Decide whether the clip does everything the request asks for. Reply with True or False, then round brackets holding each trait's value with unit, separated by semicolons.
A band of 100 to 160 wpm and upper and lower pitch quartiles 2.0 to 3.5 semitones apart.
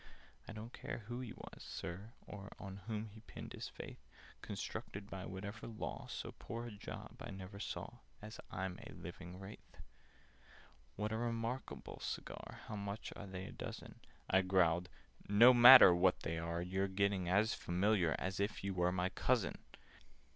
False (170 wpm; 2.9 semitones)